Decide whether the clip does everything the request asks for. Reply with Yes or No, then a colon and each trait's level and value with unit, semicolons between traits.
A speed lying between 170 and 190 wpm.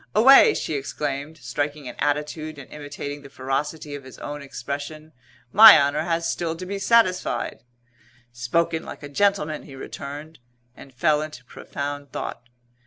No: average, 150 wpm